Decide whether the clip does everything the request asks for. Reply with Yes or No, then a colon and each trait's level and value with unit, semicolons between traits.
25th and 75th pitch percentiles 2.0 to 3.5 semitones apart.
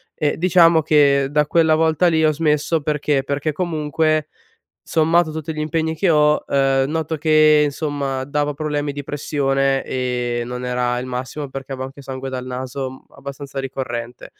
Yes: narrow, 2.6 semitones